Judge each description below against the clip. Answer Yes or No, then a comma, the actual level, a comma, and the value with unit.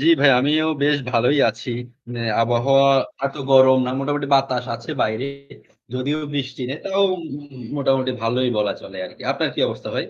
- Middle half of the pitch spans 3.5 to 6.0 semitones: No, narrow, 2.5 semitones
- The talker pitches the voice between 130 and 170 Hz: Yes, low, 135 Hz